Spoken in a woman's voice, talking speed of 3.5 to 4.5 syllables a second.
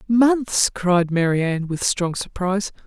Yes: female; 3.9 syllables/s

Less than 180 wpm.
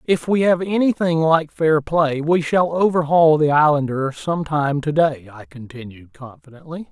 Yes: average, 155 wpm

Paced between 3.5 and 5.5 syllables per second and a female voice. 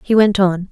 Yes: 4.9 syllables/s; female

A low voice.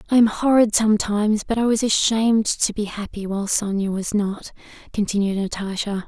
No: high, 210 Hz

